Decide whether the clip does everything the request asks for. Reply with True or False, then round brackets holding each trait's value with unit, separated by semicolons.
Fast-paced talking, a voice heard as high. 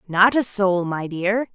False (195 wpm; 200 Hz)